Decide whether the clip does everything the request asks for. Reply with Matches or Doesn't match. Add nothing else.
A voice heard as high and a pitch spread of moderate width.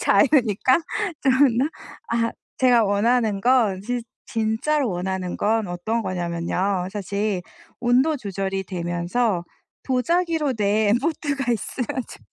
Matches